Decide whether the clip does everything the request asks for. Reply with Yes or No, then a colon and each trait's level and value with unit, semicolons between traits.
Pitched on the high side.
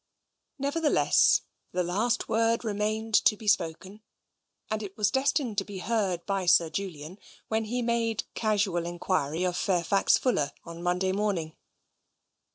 Yes: high, 200 Hz